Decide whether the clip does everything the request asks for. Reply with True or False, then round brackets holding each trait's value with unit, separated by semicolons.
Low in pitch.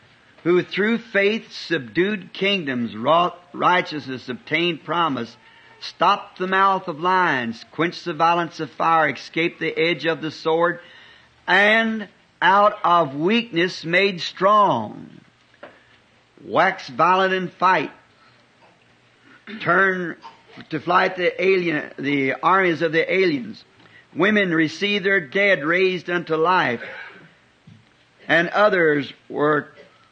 False (175 Hz)